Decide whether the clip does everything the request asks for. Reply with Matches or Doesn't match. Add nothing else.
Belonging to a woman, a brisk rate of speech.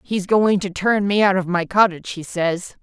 Matches